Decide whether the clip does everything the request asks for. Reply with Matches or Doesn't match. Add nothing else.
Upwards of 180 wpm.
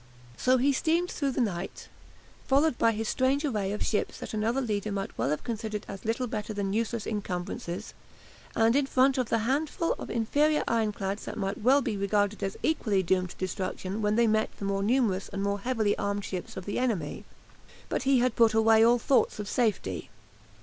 Matches